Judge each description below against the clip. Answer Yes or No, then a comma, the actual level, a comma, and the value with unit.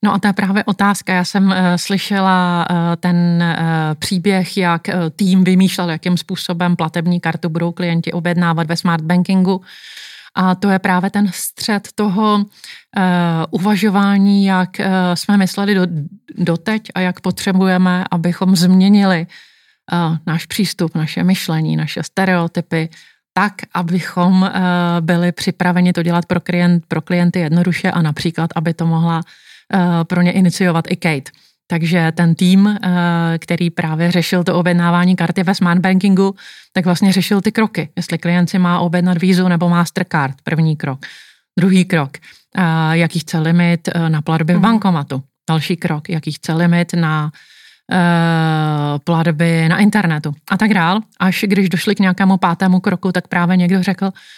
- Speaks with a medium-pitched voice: Yes, medium, 180 Hz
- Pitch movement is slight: Yes, narrow, 2.0 semitones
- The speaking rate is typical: Yes, average, 140 wpm